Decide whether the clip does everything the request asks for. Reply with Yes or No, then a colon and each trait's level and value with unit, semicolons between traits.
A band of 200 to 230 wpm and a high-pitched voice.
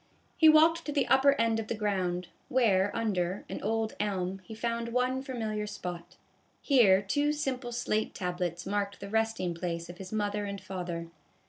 No: average, 170 wpm; high, 210 Hz